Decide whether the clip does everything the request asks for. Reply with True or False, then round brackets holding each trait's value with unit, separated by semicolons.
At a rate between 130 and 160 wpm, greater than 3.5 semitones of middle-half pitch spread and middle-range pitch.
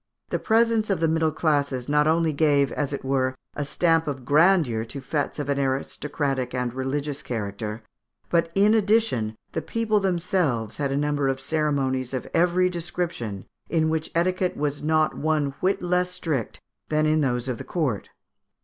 False (170 wpm; 4.3 semitones; 150 Hz)